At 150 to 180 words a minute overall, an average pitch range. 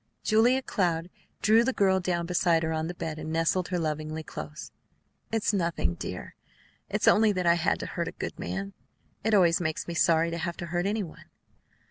No: fast, 205 wpm; average, 3.1 semitones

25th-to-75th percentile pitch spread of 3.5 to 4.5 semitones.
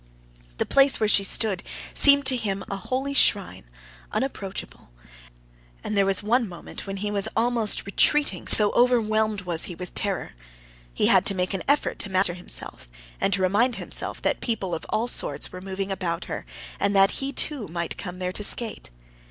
Yes: average, 4.0 semitones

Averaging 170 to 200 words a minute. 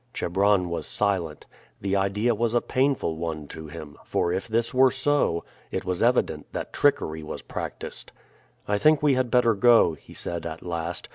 Yes: average, 180 wpm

